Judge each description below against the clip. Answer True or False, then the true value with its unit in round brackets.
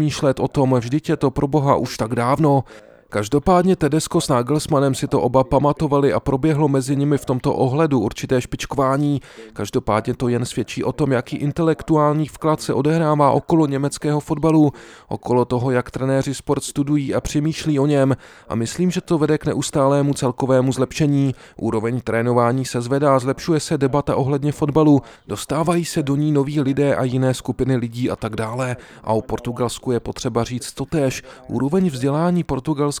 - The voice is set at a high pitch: False (140 Hz)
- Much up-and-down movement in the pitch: False (2.8 semitones)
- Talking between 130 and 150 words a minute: False (165 wpm)